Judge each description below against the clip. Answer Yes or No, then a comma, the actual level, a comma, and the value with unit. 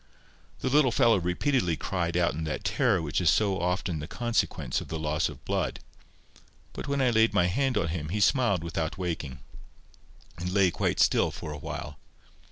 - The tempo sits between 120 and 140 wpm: No, average, 190 wpm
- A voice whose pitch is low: Yes, very low, 90 Hz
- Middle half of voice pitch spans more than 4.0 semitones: Yes, wide, 5.6 semitones